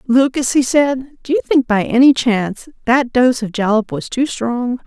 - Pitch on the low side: No, very high, 250 Hz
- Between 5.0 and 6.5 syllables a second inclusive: No, 4.6 syllables/s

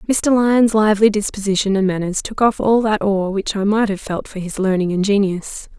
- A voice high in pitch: Yes, high, 205 Hz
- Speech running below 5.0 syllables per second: No, 5.3 syllables/s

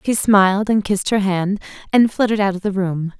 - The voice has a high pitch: Yes, high, 200 Hz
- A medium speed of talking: No, fast, 225 wpm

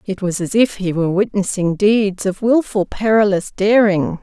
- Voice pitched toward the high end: Yes, high, 200 Hz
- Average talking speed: Yes, average, 170 wpm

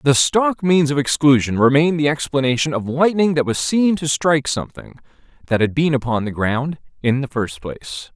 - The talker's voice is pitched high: No, medium, 140 Hz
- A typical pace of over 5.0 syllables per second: Yes, 5.3 syllables/s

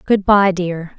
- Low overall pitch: No, medium, 185 Hz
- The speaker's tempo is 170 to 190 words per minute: Yes, average, 185 wpm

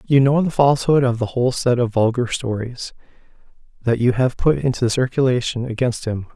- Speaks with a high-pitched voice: No, low, 125 Hz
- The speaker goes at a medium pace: Yes, average, 180 wpm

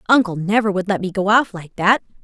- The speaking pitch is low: No, high, 200 Hz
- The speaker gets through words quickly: Yes, fast, 240 wpm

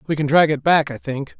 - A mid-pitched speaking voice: Yes, medium, 150 Hz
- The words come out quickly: Yes, fast, 300 wpm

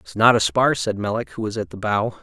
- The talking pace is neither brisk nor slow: No, fast, 295 wpm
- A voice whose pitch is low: Yes, low, 110 Hz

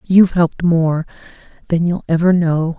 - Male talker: No, female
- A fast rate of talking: No, slow, 130 wpm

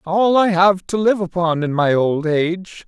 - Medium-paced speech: No, fast, 210 wpm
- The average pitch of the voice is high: No, medium, 180 Hz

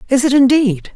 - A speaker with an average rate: Yes, average, 190 wpm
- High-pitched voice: Yes, very high, 255 Hz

